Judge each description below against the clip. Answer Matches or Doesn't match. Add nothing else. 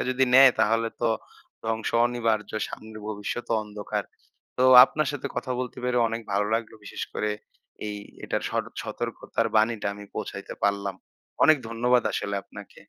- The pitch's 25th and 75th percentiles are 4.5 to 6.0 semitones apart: Doesn't match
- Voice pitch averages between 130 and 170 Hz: Doesn't match